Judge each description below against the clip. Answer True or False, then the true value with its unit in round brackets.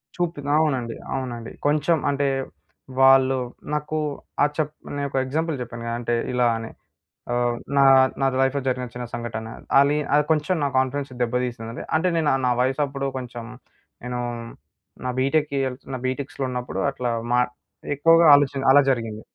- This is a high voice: False (135 Hz)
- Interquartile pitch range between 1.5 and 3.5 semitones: True (2.9 semitones)